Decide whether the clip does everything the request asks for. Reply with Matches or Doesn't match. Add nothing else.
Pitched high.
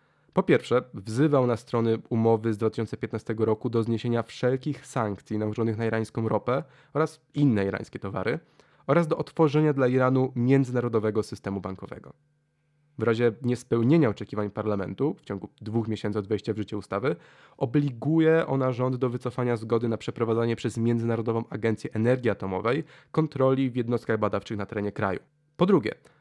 Doesn't match